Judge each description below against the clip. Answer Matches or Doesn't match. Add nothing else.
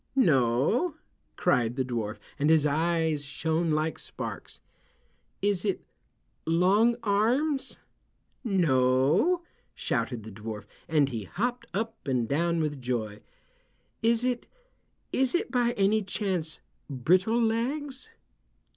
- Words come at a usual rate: Doesn't match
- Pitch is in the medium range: Matches